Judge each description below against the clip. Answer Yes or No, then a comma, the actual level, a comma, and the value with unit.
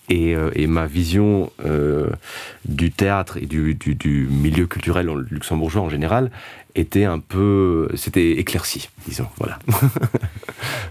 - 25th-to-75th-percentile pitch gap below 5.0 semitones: Yes, average, 4.5 semitones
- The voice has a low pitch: Yes, very low, 90 Hz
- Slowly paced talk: Yes, slow, 125 wpm